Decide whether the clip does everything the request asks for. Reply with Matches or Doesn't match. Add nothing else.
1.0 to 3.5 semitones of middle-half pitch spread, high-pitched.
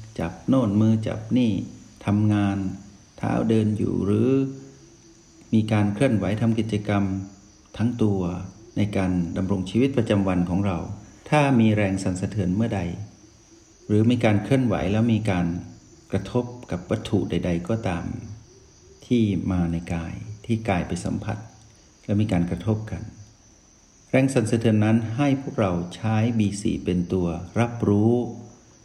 Doesn't match